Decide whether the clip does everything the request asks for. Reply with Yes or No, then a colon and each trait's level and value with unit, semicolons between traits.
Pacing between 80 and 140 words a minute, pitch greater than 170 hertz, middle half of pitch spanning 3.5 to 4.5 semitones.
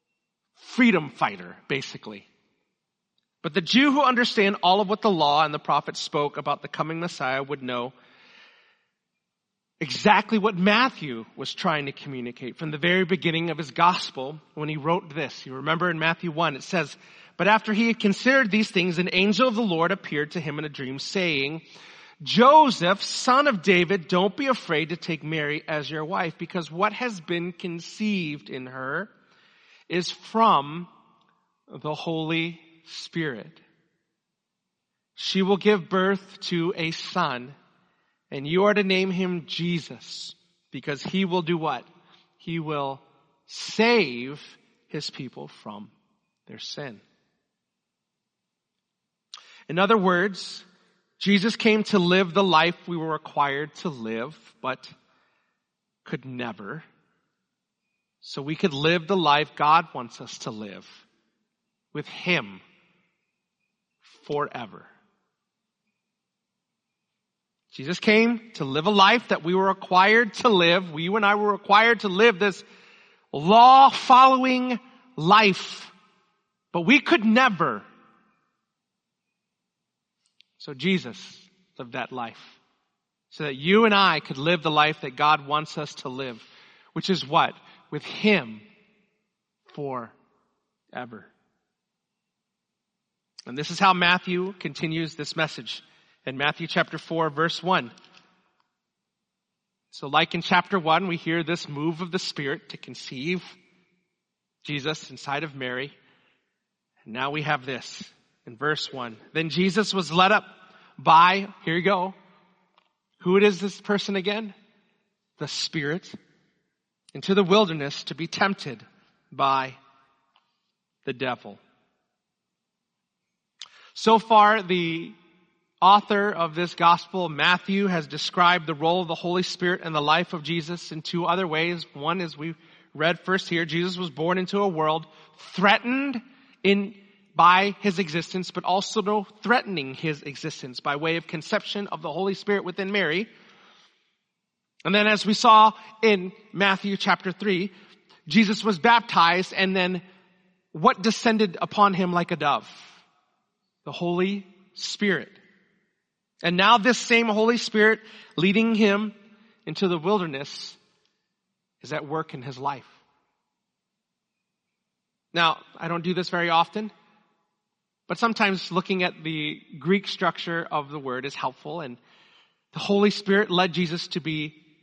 Yes: slow, 135 wpm; medium, 185 Hz; average, 4.2 semitones